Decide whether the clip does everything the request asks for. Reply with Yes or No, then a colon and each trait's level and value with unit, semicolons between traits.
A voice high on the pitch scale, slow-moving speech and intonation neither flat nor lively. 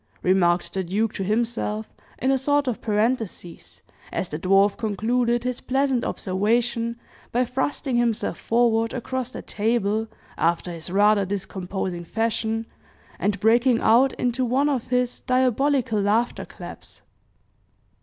Yes: high, 225 Hz; slow, 130 wpm; average, 3.5 semitones